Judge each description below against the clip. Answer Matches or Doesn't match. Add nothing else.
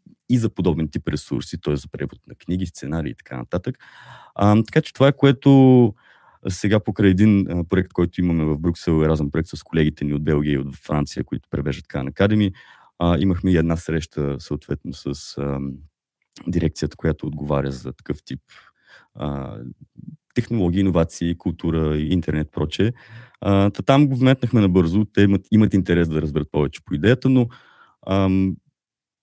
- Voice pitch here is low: Matches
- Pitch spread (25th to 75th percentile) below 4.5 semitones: Doesn't match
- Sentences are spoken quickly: Matches